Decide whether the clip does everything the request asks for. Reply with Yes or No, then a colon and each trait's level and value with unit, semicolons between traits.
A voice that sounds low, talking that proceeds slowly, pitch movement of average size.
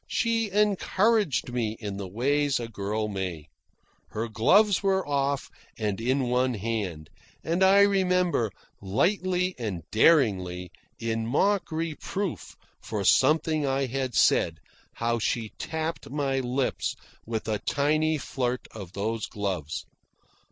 No: low, 130 Hz; slow, 125 wpm; wide, 7.1 semitones